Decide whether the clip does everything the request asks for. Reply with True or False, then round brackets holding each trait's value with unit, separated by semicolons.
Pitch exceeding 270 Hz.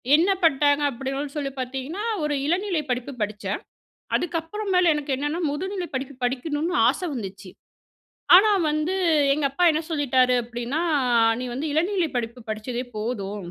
True (285 Hz)